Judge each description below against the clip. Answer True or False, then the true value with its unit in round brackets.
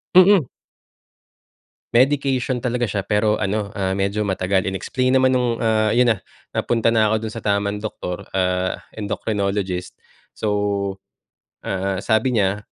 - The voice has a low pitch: True (105 Hz)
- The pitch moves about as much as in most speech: True (3.7 semitones)